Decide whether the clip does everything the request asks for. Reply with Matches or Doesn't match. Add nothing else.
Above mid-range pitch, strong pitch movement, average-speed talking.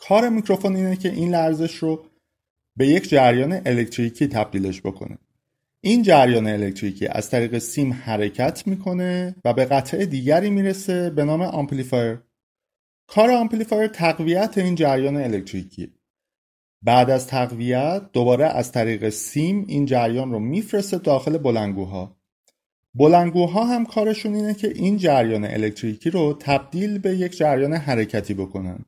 Doesn't match